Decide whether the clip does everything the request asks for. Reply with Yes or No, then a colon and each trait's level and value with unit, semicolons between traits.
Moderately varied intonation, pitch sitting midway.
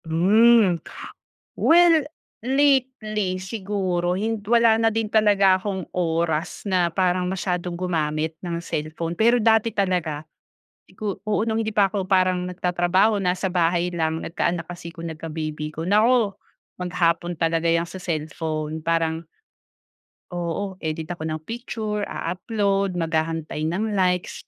Yes: average, 3.9 semitones; medium, 180 Hz